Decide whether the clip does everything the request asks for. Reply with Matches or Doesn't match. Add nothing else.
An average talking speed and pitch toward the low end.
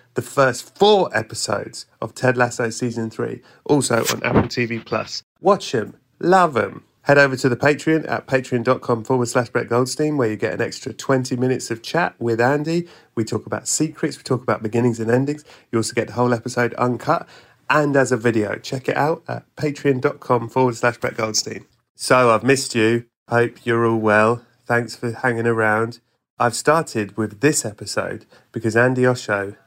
Matches